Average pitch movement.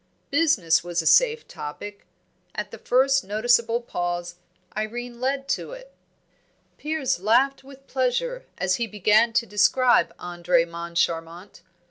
No: wide, 7.4 semitones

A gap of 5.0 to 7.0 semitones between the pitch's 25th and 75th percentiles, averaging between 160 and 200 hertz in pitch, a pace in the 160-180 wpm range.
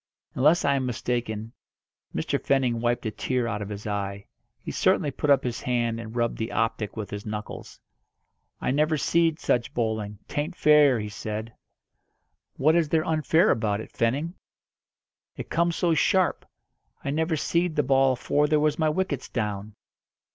No: wide, 5.6 semitones; low, 125 Hz; average, 170 wpm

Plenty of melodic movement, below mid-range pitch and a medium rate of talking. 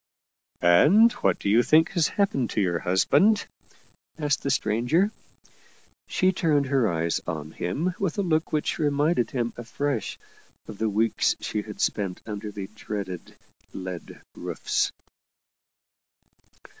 Yes: wide, 7.7 semitones; low, 120 Hz; average, 145 wpm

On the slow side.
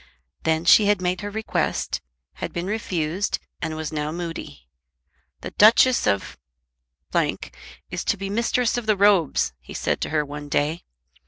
No: average, 155 wpm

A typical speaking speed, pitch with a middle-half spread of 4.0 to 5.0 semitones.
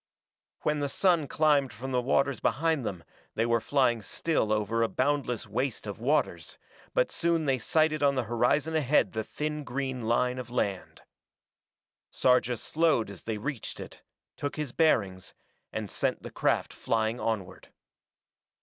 Yes: average, 155 wpm; average, 4.7 semitones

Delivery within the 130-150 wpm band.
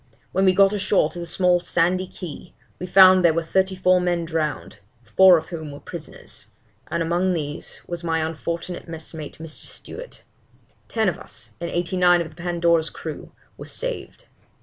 No: average, 175 wpm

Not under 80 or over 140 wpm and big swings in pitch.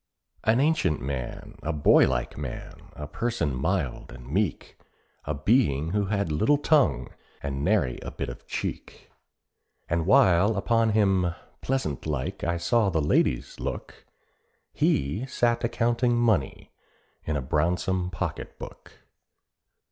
Yes: slow, 135 wpm; wide, 7.7 semitones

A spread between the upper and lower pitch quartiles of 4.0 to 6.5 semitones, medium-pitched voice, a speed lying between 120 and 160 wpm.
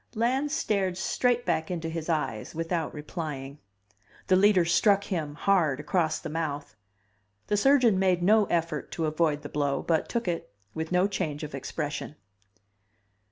Yes: average, 4.3 semitones; medium, 165 Hz; average, 155 wpm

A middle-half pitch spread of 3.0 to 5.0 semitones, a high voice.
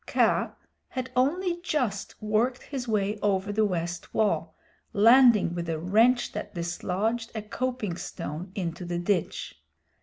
No: wide, 5.5 semitones; high, 210 Hz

